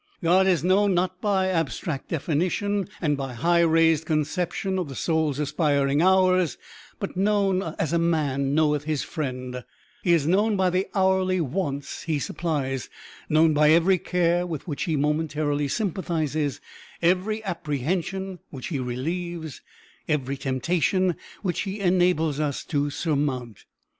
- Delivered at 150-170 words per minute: No, average, 140 wpm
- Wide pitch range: No, average, 4.1 semitones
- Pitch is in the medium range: Yes, medium, 165 Hz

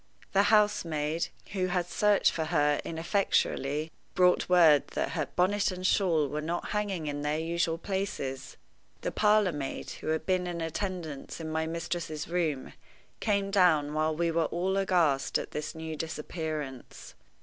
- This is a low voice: No, medium, 165 Hz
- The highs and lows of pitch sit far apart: No, average, 3.2 semitones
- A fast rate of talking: No, average, 155 wpm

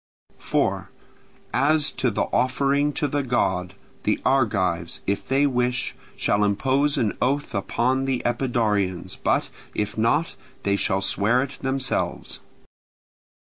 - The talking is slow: Yes, slow, 125 wpm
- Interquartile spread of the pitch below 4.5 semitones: No, average, 4.9 semitones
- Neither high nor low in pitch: No, low, 125 Hz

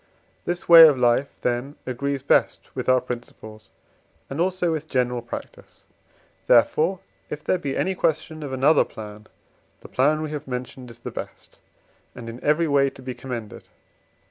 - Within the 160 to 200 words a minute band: Yes, average, 165 wpm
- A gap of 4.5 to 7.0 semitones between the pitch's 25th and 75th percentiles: No, average, 4.0 semitones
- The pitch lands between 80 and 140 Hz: Yes, low, 135 Hz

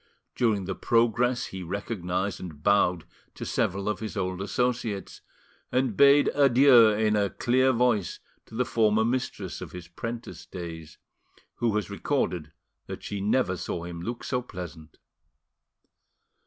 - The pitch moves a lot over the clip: No, average, 4.7 semitones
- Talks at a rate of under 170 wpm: Yes, average, 140 wpm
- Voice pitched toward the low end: Yes, low, 105 Hz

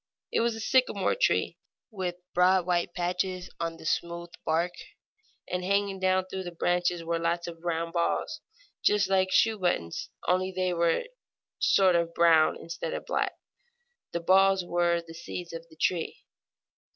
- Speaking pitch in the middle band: Yes, medium, 175 Hz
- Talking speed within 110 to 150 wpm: No, average, 165 wpm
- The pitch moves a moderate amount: No, narrow, 1.9 semitones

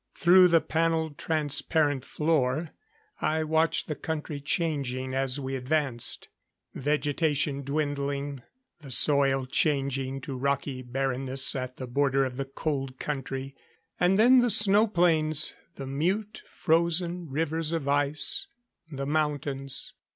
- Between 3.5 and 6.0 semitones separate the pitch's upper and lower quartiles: No, average, 3.0 semitones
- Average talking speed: No, slow, 120 wpm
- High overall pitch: No, medium, 145 Hz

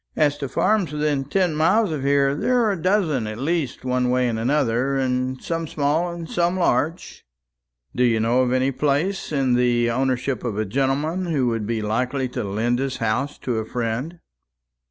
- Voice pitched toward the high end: No, low, 135 Hz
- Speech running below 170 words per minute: No, average, 185 wpm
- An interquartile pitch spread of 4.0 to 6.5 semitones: Yes, average, 4.5 semitones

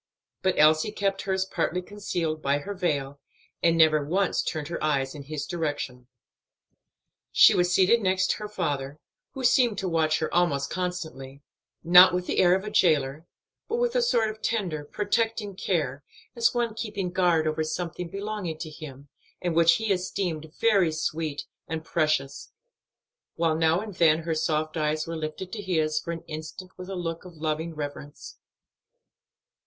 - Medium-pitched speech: Yes, medium, 165 Hz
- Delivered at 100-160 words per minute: No, average, 170 wpm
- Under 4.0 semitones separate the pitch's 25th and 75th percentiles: Yes, average, 3.5 semitones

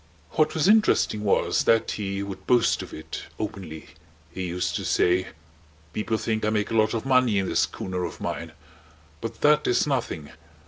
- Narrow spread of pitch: No, average, 4.3 semitones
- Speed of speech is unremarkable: Yes, average, 180 wpm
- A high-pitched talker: No, low, 105 Hz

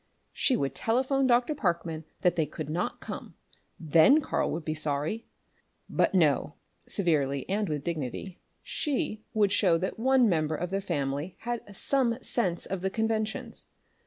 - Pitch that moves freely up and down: Yes, wide, 6.3 semitones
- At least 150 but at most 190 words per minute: Yes, average, 155 wpm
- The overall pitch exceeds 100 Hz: Yes, medium, 185 Hz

